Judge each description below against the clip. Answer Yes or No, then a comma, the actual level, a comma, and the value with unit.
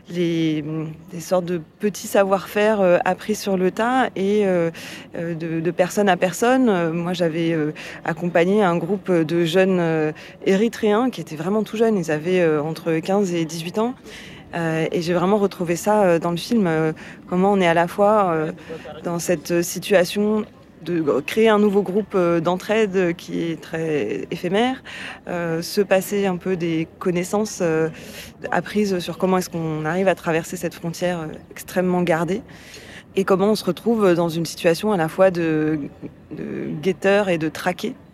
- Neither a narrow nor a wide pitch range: Yes, average, 3.2 semitones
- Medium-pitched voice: Yes, medium, 180 Hz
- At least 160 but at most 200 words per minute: Yes, average, 170 wpm